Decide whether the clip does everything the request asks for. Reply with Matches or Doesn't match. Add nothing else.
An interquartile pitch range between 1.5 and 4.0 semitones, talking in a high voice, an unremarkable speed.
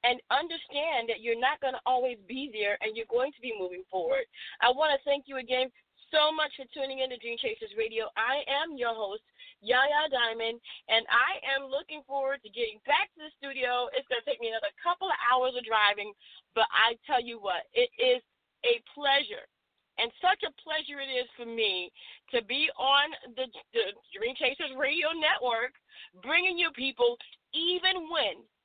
Doesn't match